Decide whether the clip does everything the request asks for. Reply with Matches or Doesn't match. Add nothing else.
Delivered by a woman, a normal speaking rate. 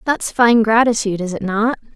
Matches